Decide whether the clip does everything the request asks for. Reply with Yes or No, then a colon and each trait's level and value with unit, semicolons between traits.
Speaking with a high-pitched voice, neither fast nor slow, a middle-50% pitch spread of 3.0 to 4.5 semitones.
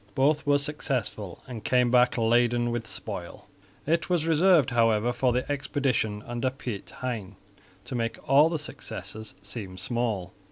No: low, 120 Hz; average, 150 wpm; average, 4.1 semitones